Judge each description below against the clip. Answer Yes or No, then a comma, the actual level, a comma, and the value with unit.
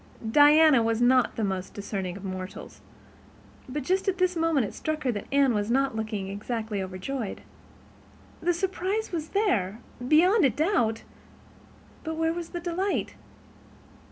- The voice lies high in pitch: Yes, very high, 270 Hz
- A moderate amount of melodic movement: No, wide, 7.9 semitones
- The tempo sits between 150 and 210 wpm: No, average, 140 wpm